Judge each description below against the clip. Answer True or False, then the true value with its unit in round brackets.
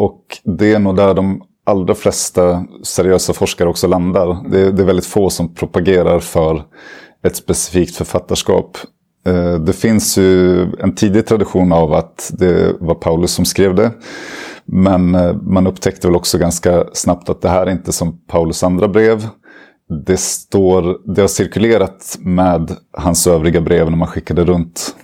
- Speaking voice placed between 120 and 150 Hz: False (90 Hz)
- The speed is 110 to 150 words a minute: False (160 wpm)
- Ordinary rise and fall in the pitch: False (1.7 semitones)